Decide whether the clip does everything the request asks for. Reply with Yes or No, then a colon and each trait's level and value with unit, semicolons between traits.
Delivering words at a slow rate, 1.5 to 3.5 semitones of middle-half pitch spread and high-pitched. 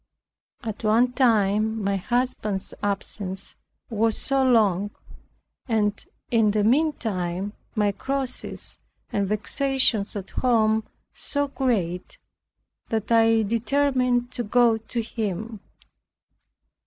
Yes: slow, 100 wpm; average, 3.2 semitones; high, 220 Hz